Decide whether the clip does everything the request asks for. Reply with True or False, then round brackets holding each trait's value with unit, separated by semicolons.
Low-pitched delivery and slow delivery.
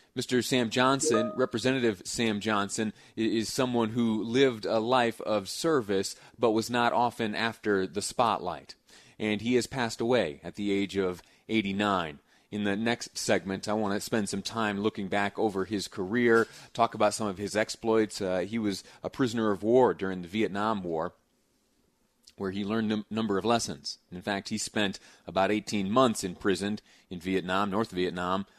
False (110 Hz; 175 wpm)